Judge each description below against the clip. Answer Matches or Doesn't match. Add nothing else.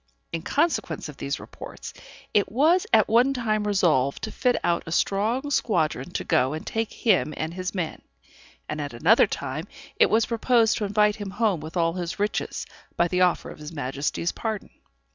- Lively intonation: Matches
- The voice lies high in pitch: Matches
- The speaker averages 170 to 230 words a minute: Matches